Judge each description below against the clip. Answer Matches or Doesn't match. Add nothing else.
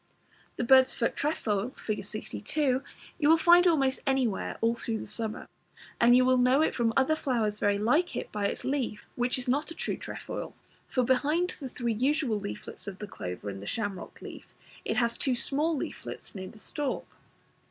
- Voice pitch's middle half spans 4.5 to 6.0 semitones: Matches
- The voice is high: Matches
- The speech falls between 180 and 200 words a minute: Matches